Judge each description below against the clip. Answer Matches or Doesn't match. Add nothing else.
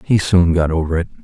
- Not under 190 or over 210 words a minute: Doesn't match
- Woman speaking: Doesn't match